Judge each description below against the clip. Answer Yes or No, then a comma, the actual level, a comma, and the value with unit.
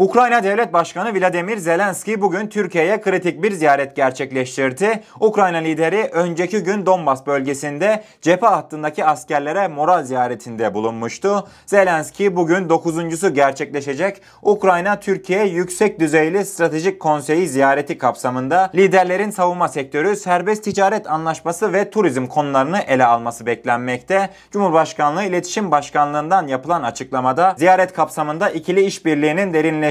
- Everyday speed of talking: Yes, average, 115 wpm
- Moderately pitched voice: Yes, medium, 170 Hz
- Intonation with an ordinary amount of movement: Yes, average, 4.9 semitones